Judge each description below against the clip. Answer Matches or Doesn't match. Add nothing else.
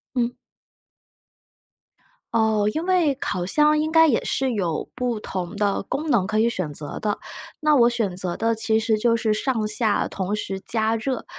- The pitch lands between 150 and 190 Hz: Doesn't match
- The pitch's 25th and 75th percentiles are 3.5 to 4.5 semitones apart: Matches